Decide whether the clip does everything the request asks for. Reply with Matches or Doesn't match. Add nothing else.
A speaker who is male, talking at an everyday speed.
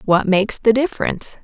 Doesn't match